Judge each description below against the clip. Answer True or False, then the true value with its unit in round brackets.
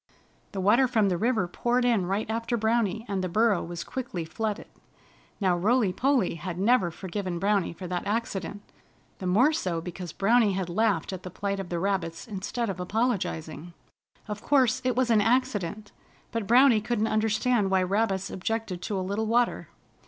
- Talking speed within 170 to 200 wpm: True (175 wpm)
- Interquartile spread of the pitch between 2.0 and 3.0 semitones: False (3.9 semitones)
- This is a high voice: True (205 Hz)